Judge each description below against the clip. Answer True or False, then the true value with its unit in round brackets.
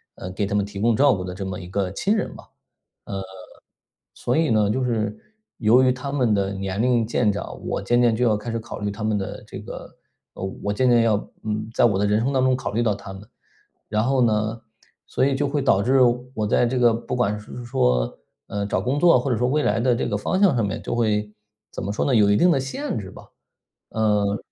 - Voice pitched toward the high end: False (110 Hz)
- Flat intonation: False (3.7 semitones)